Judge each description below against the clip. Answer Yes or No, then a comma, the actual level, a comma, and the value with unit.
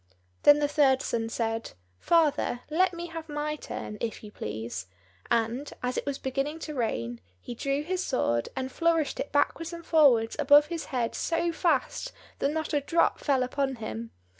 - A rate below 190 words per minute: Yes, average, 180 wpm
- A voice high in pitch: Yes, very high, 280 Hz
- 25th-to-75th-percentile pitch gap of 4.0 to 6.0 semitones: Yes, average, 5.1 semitones